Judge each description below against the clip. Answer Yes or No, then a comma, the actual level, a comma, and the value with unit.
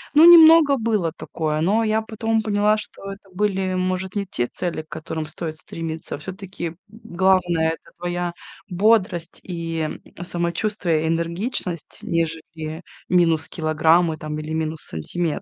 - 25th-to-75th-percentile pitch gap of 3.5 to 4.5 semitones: Yes, average, 3.8 semitones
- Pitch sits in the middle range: Yes, medium, 175 Hz